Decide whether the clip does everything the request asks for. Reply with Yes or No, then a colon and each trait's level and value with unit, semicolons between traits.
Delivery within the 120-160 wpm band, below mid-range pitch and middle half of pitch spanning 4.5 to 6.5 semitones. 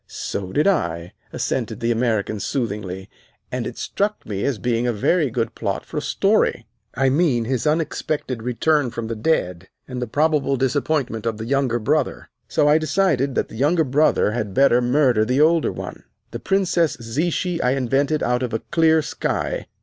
No: average, 180 wpm; low, 130 Hz; average, 5.0 semitones